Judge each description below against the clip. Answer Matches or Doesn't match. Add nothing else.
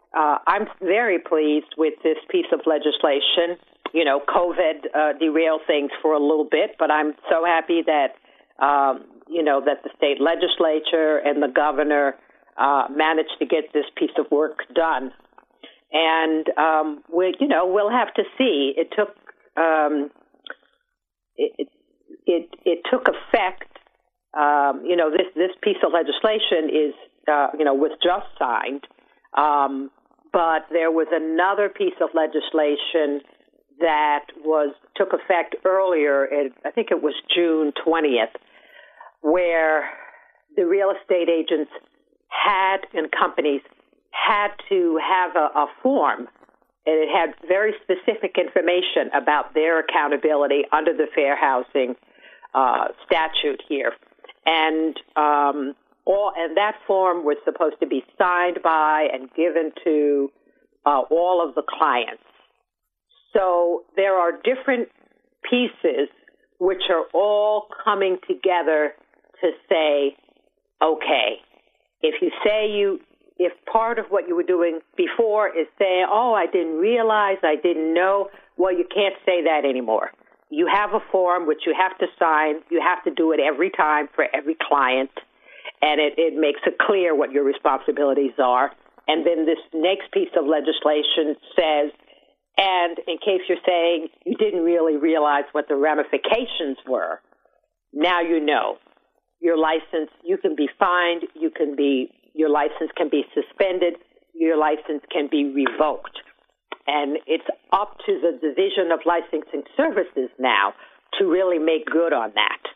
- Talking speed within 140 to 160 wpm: Matches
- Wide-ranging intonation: Doesn't match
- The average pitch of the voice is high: Doesn't match